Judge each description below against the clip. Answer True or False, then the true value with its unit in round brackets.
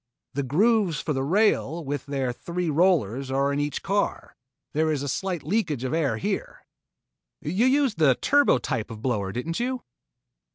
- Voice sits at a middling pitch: True (150 Hz)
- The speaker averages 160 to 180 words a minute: True (170 wpm)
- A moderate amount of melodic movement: False (6.0 semitones)